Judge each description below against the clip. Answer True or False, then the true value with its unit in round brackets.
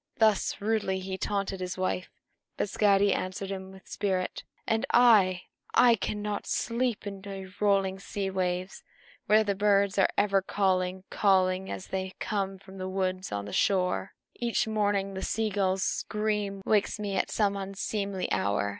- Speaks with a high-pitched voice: True (195 Hz)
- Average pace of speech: True (160 wpm)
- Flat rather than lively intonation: True (1.6 semitones)